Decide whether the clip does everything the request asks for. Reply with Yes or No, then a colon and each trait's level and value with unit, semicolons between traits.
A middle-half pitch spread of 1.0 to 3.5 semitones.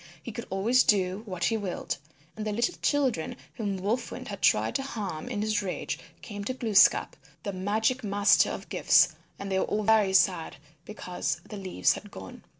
Yes: average, 2.8 semitones